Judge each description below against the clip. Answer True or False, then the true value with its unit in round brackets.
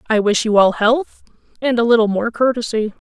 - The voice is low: False (230 Hz)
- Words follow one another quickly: False (195 wpm)